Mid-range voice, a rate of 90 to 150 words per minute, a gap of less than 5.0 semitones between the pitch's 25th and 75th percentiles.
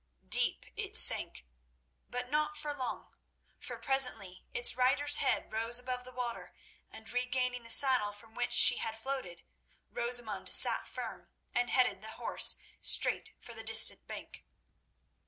No: high, 245 Hz; average, 145 wpm; average, 2.8 semitones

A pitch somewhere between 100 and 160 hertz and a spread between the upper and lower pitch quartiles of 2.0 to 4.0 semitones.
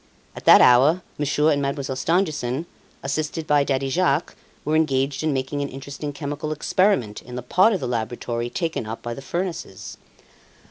Yes: medium, 140 Hz; average, 3.2 semitones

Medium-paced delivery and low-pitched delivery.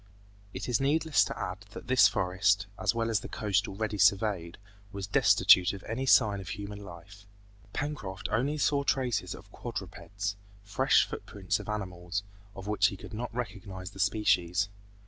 Yes: average, 165 wpm; low, 100 Hz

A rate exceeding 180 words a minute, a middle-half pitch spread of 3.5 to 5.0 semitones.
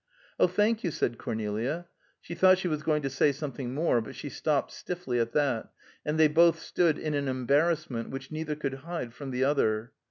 Yes: average, 200 wpm; average, 4.3 semitones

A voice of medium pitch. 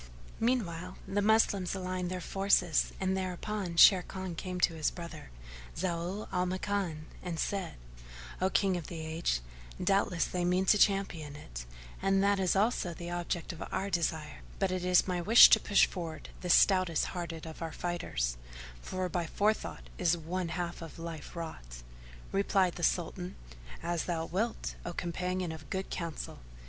Yes: medium, 180 Hz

